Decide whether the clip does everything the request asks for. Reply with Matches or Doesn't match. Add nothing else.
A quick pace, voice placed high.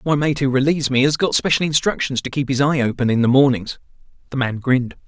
Doesn't match